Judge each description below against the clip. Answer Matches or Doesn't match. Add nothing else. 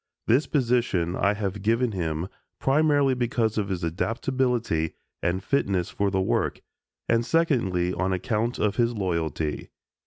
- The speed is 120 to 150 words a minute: Matches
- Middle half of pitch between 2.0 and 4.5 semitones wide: Doesn't match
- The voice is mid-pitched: Doesn't match